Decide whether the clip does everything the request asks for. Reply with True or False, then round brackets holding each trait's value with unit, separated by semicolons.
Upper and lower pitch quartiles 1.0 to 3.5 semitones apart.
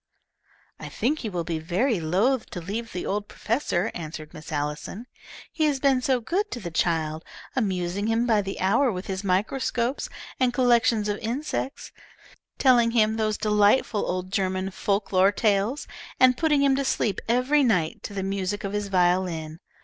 False (4.9 semitones)